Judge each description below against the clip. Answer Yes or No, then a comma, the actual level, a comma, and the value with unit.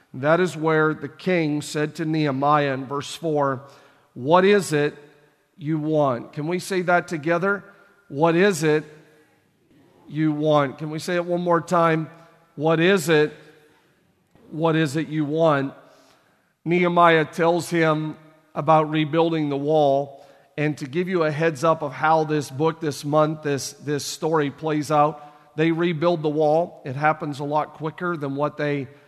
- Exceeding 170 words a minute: No, average, 160 wpm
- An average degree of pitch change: No, narrow, 2.0 semitones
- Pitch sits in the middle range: Yes, medium, 155 Hz